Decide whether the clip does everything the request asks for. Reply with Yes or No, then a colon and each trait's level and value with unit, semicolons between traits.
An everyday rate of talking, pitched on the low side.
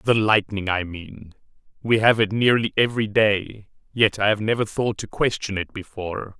Yes: average, 180 wpm; low, 105 Hz